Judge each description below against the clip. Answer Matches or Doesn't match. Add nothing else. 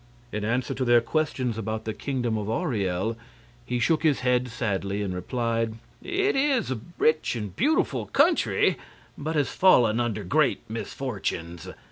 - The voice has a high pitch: Doesn't match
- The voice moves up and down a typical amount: Matches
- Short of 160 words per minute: Matches